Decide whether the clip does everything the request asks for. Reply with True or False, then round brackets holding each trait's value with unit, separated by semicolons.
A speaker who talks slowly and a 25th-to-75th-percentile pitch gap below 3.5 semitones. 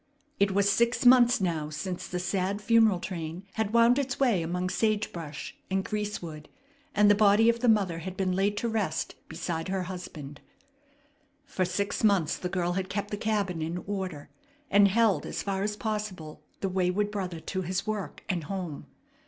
False (180 wpm; 2.9 semitones)